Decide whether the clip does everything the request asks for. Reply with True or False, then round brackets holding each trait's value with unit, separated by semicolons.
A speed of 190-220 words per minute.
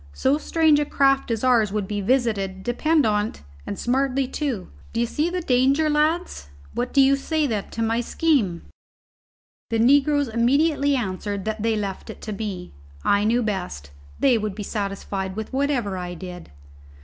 False (170 wpm)